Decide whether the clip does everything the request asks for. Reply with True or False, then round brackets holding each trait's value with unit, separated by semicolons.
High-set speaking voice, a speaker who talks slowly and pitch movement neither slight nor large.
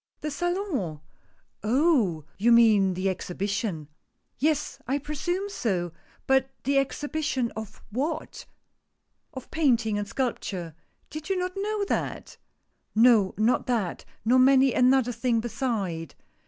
False (250 Hz; 125 wpm; 6.1 semitones)